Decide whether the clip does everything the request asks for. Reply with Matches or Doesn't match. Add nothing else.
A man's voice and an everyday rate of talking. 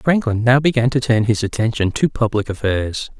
Matches